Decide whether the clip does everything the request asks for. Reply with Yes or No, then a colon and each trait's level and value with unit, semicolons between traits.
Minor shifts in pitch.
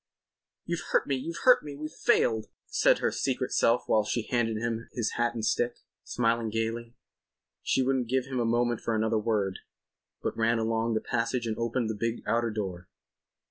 Yes: narrow, 1.5 semitones